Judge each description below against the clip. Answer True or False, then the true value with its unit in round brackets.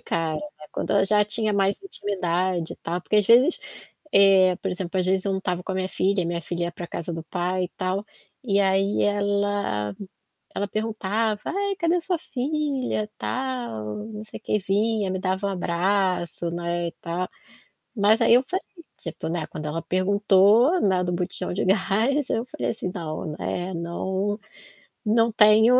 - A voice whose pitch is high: True (195 Hz)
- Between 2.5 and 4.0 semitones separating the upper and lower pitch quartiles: True (3.3 semitones)